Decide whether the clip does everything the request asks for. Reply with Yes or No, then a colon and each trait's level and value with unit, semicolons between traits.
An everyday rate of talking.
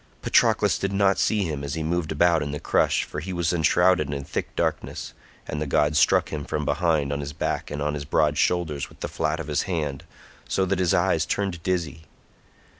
No: fast, 210 wpm